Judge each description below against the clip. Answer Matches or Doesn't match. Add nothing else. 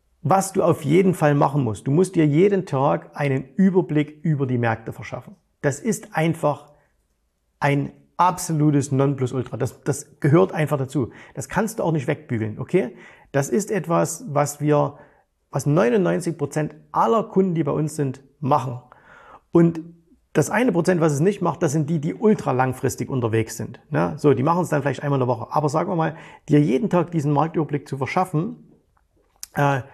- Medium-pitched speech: Matches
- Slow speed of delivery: Doesn't match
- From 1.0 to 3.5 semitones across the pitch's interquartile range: Doesn't match